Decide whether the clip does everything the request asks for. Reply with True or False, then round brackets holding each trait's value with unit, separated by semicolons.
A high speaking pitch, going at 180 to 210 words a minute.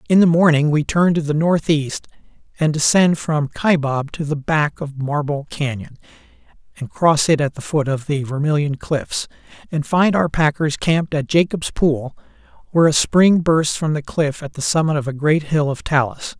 False (150 Hz; 190 wpm)